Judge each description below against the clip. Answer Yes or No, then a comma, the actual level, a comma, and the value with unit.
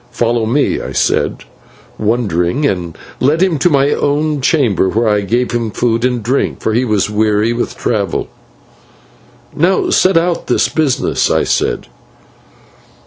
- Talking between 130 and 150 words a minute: Yes, average, 145 wpm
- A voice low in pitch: Yes, low, 120 Hz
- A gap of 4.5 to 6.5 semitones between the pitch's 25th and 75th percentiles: Yes, average, 5.2 semitones